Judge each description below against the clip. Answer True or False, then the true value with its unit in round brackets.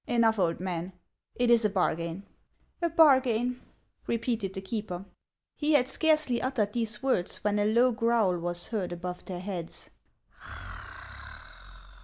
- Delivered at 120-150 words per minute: True (145 wpm)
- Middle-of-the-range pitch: False (215 Hz)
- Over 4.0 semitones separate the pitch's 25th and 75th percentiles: True (5.1 semitones)